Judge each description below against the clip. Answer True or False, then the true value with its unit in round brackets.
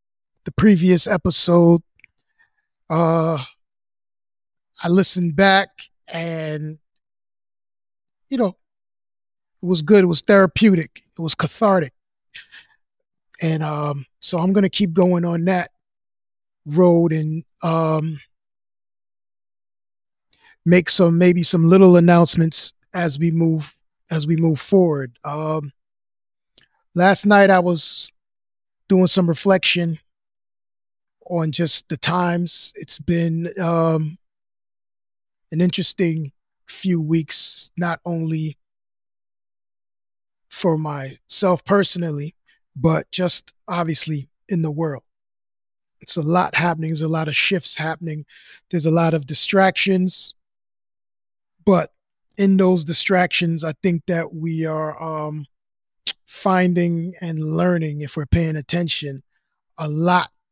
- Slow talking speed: True (110 wpm)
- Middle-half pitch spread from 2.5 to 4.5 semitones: True (3.4 semitones)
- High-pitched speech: False (165 Hz)